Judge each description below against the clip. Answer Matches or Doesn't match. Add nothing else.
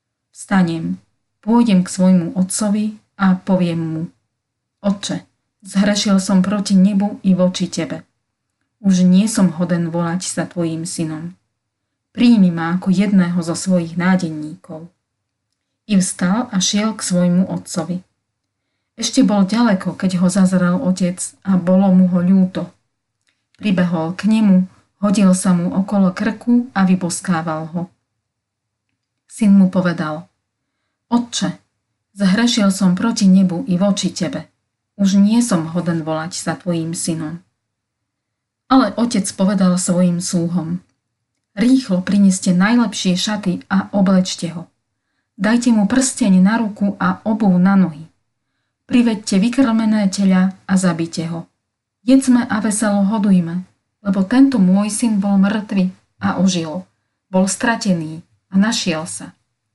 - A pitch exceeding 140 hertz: Matches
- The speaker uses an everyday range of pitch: Matches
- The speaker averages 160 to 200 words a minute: Doesn't match